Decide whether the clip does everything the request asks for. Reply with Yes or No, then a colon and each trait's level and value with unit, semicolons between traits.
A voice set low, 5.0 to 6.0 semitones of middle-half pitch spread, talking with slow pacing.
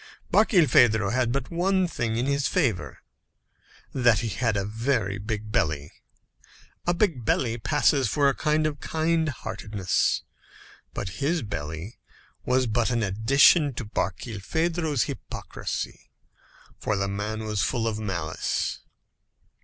Yes: low, 120 Hz; wide, 5.5 semitones; slow, 130 wpm